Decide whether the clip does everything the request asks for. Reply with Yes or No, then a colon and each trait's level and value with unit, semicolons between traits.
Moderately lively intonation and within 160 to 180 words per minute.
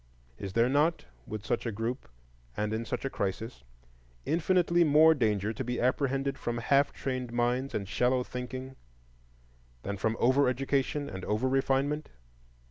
No: average, 3.4 semitones; average, 150 wpm